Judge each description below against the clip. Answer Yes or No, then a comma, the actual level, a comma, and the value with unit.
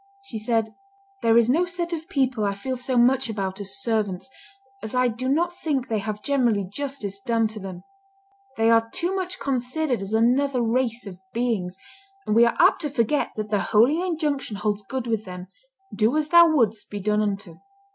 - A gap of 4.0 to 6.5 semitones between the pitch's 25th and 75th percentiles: Yes, average, 4.6 semitones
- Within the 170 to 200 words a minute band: Yes, average, 195 wpm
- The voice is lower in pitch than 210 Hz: No, high, 235 Hz